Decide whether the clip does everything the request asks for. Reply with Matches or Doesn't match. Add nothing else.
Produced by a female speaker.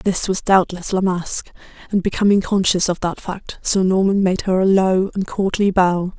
Matches